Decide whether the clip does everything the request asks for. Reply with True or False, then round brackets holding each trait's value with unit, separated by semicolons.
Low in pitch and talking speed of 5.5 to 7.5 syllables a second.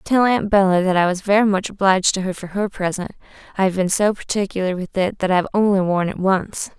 False (190 Hz; 6.0 syllables/s)